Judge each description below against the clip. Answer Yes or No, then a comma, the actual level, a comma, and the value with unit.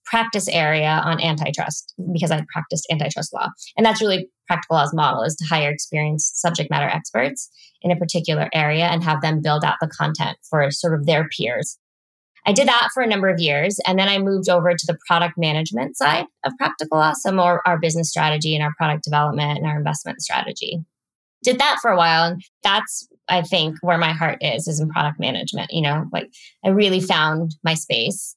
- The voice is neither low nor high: Yes, medium, 165 Hz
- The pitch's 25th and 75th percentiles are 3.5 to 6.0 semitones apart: No, narrow, 2.6 semitones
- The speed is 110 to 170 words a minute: No, fast, 205 wpm